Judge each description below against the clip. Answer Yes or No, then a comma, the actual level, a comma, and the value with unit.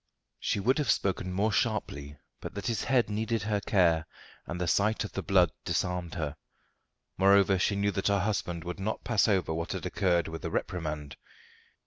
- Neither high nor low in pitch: No, very low, 95 Hz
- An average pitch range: Yes, average, 3.2 semitones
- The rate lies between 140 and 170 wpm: No, average, 185 wpm